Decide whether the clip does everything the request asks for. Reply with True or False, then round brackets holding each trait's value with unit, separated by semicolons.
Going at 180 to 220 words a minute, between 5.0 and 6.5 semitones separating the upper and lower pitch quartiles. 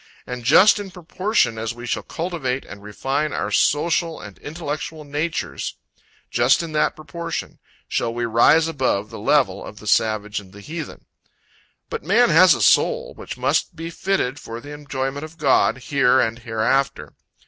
False (165 wpm; 5.6 semitones)